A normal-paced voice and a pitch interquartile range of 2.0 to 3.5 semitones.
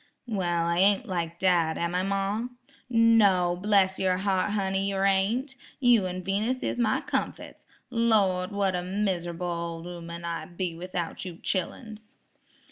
Yes: average, 150 wpm; average, 2.9 semitones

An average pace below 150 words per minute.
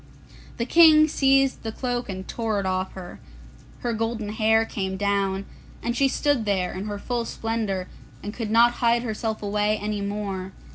No: average, 175 wpm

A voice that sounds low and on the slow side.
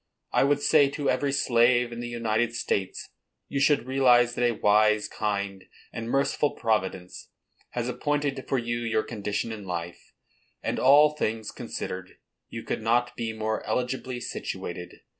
No: low, 120 Hz; average, 155 wpm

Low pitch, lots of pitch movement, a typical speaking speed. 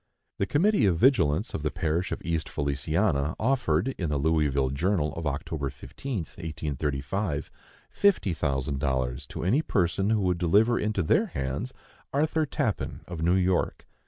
Yes: very low, 85 Hz; wide, 6.2 semitones; average, 155 wpm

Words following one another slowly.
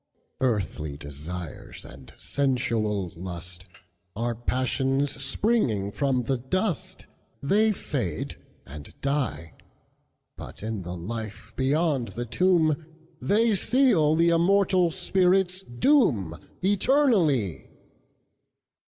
Yes: slow, 75 wpm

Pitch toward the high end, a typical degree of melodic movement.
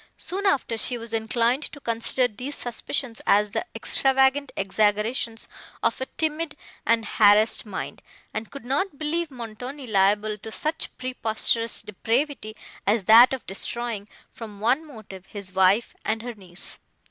Yes: high, 230 Hz; average, 3.9 semitones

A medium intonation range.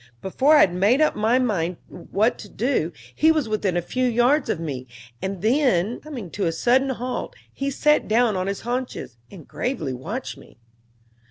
No: wide, 6.0 semitones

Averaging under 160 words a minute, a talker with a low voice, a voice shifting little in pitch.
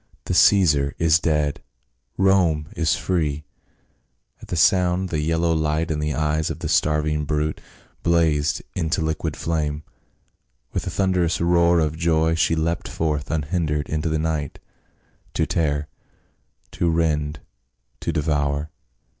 Yes: average, 140 wpm; very low, 80 Hz; narrow, 1.8 semitones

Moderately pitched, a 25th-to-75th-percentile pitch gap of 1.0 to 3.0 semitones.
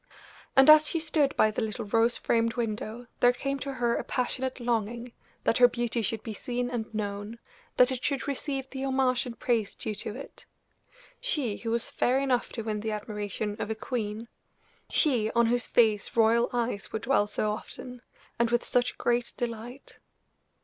No: high, 235 Hz; narrow, 2.5 semitones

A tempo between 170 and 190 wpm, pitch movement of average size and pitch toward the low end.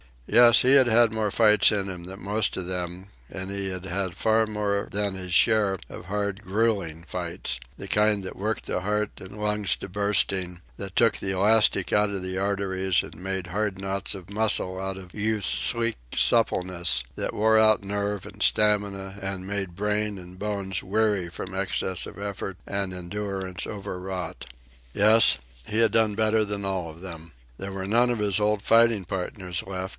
No: average, 185 wpm; narrow, 2.2 semitones; low, 100 Hz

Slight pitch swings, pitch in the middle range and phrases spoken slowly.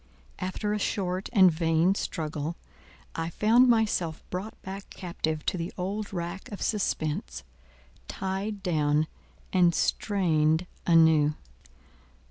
No: average, 3.8 semitones; medium, 180 Hz; slow, 110 wpm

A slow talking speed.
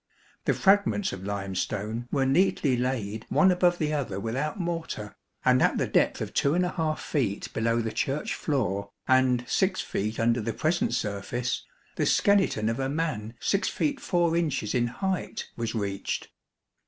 No: average, 155 wpm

